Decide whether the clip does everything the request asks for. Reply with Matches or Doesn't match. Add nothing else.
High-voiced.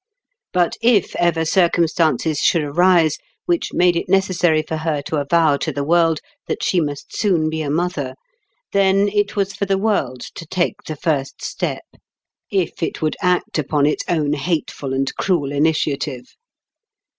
Doesn't match